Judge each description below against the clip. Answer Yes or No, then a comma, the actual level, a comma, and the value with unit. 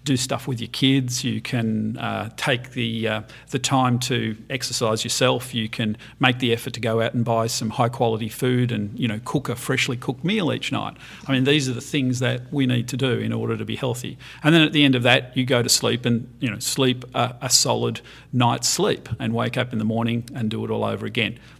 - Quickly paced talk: Yes, fast, 245 wpm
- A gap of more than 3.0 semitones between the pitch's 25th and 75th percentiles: No, narrow, 2.5 semitones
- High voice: No, low, 120 Hz